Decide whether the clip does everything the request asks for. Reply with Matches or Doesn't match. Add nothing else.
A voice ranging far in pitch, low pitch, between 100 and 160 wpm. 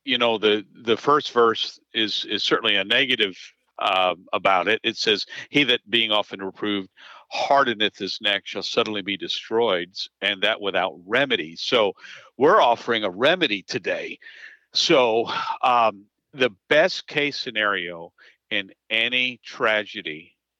Matches